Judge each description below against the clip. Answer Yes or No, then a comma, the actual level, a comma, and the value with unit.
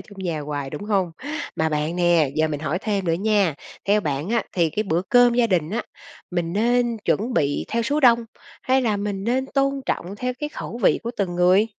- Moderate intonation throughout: No, wide, 5.9 semitones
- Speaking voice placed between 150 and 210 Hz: Yes, high, 200 Hz